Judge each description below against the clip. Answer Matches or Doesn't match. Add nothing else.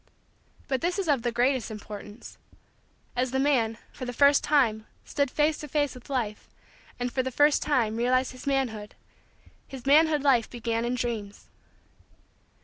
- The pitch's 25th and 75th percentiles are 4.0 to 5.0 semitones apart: Doesn't match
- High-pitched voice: Matches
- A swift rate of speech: Doesn't match